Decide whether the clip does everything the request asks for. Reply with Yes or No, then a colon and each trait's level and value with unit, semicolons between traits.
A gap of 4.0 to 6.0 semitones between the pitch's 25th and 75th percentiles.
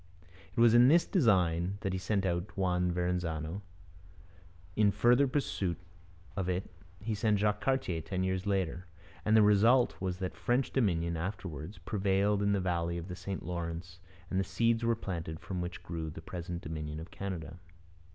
No: average, 3.3 semitones